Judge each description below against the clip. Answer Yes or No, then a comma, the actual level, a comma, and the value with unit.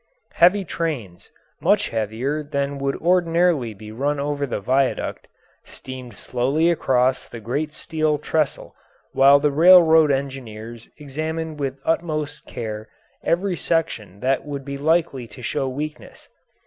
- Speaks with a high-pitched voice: No, medium, 140 Hz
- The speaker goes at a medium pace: No, slow, 130 wpm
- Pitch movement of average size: Yes, average, 3.9 semitones